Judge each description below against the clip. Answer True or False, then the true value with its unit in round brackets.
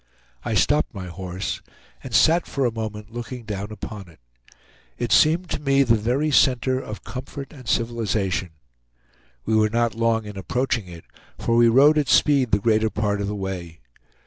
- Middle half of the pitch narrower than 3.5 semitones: False (4.0 semitones)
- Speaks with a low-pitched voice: True (115 Hz)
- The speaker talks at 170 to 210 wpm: True (175 wpm)